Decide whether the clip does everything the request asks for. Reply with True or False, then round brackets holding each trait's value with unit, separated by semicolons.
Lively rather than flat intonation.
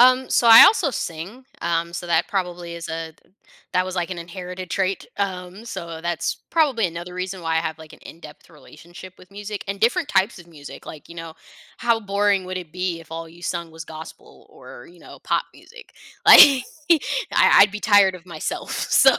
False (3.1 semitones)